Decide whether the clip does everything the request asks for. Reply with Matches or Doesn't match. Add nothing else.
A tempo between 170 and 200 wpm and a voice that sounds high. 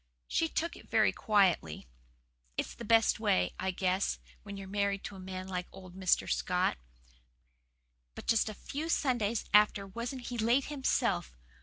Doesn't match